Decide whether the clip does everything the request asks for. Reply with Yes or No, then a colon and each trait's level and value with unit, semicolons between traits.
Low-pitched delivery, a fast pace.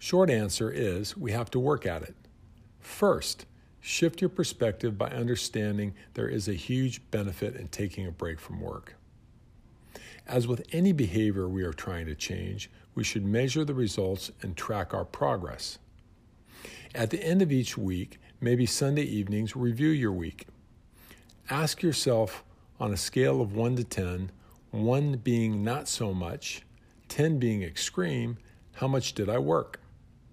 No: low, 115 Hz; average, 155 wpm